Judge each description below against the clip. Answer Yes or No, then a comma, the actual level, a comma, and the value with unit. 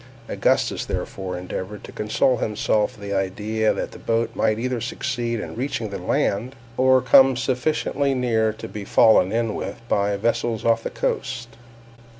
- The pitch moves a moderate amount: Yes, average, 3.2 semitones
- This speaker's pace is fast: No, average, 160 wpm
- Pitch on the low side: Yes, low, 115 Hz